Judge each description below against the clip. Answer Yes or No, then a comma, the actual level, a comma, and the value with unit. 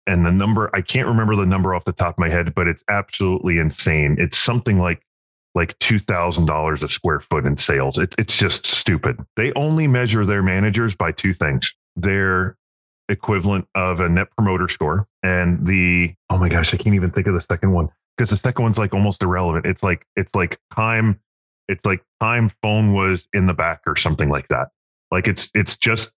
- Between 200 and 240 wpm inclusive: Yes, fast, 205 wpm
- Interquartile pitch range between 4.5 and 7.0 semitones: No, average, 3.3 semitones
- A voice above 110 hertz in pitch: No, very low, 95 Hz